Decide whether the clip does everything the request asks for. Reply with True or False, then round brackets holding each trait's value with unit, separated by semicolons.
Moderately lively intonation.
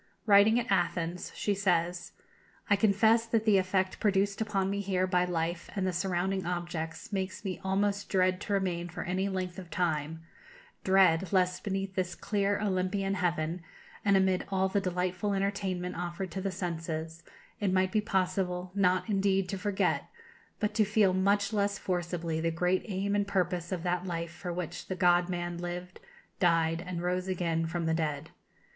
False (2.1 semitones)